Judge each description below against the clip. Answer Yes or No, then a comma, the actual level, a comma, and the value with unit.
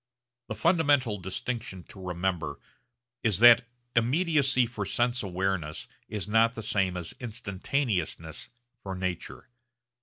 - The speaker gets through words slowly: Yes, slow, 115 wpm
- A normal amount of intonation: Yes, average, 4.8 semitones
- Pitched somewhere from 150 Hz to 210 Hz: No, low, 105 Hz